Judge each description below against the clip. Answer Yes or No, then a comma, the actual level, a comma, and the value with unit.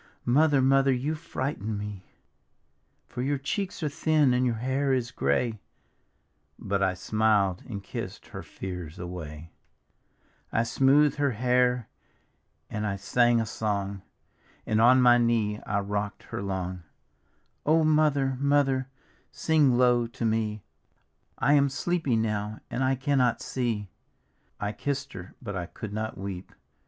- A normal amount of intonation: Yes, average, 4.8 semitones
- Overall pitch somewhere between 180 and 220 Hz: No, low, 120 Hz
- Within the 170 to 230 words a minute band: No, average, 150 wpm